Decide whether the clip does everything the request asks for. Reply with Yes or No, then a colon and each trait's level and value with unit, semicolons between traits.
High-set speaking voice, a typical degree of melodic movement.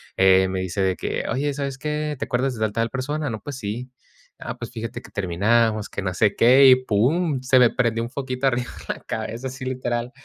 No: low, 120 Hz; average, 3.7 semitones